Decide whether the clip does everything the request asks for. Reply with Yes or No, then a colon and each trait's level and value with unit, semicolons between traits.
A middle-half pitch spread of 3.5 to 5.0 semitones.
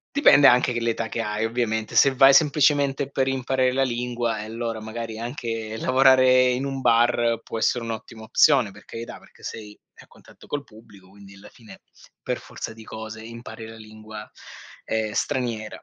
No: narrow, 2.6 semitones